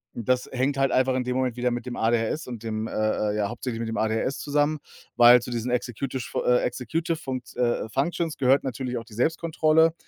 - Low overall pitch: Yes, low, 125 Hz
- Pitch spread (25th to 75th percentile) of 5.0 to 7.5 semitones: No, narrow, 2.6 semitones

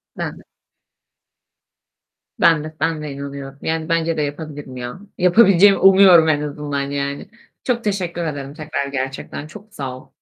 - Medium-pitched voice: Yes, medium, 155 Hz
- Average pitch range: Yes, average, 3.5 semitones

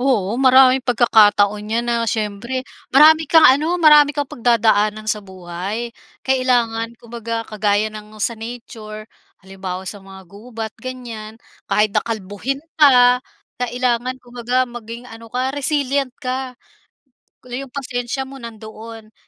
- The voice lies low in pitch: No, high, 235 Hz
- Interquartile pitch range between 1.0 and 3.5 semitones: Yes, average, 3.1 semitones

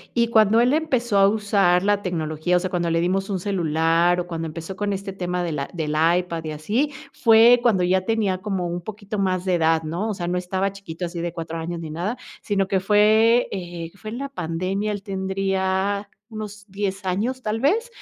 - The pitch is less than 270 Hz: Yes, high, 190 Hz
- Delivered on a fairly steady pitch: No, average, 3.3 semitones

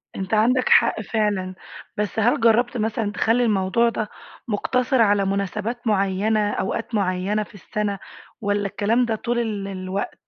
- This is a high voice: Yes, high, 210 Hz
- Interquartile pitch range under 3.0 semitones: Yes, narrow, 2.5 semitones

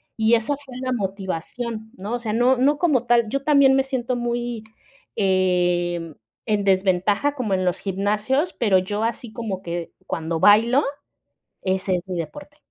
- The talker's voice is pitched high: Yes, high, 215 Hz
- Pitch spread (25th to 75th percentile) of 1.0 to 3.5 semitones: No, average, 4.6 semitones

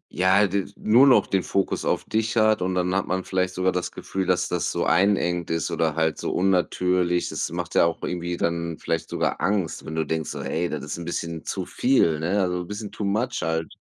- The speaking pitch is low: Yes, very low, 90 Hz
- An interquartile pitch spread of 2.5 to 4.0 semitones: Yes, average, 2.8 semitones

